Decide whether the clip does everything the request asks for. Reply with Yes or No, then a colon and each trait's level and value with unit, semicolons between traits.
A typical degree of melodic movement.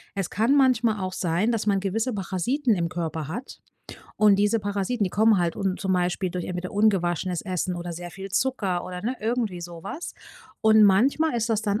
Yes: average, 3.8 semitones